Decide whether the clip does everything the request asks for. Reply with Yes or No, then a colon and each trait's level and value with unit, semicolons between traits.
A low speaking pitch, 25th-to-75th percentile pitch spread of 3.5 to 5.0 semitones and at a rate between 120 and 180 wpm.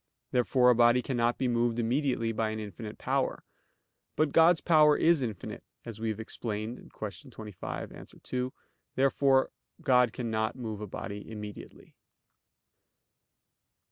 No: low, 120 Hz; average, 3.0 semitones; slow, 135 wpm